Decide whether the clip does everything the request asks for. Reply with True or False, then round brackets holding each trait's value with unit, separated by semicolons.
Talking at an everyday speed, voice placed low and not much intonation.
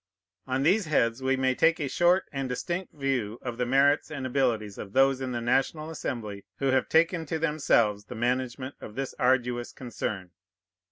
False (180 wpm; 130 Hz; 3.3 semitones)